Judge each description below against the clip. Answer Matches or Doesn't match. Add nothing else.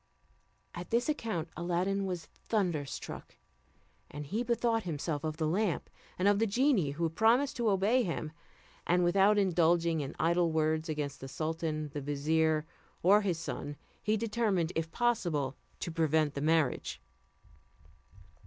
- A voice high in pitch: Doesn't match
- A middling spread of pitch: Matches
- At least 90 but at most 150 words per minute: Matches